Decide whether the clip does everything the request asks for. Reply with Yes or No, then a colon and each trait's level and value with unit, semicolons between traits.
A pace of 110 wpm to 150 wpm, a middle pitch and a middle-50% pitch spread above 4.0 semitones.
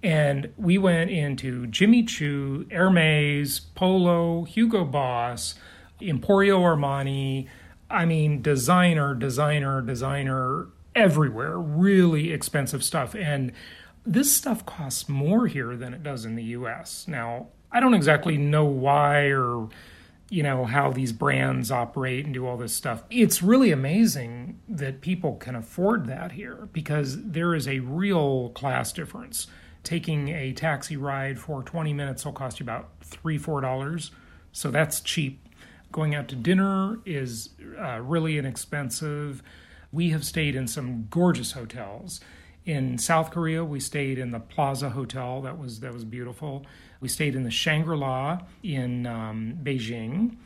Yes: average, 145 wpm; medium, 145 Hz; average, 4.5 semitones